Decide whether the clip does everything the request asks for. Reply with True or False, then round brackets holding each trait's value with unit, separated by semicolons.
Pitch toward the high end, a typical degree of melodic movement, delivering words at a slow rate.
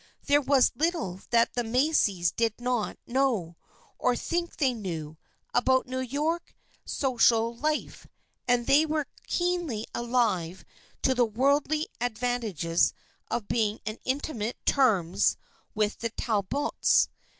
True (245 Hz; 4.6 semitones; 130 wpm)